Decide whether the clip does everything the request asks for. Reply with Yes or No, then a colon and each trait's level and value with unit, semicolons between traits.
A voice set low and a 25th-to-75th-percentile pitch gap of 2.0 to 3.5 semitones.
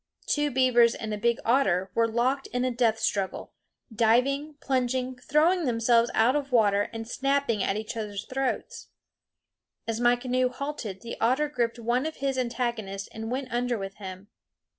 No: high, 240 Hz; average, 2.8 semitones